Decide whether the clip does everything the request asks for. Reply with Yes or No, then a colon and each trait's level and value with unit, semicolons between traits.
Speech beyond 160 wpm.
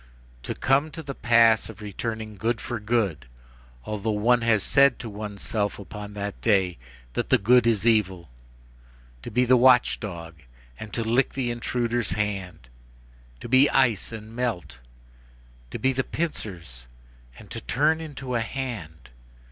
No: average, 155 wpm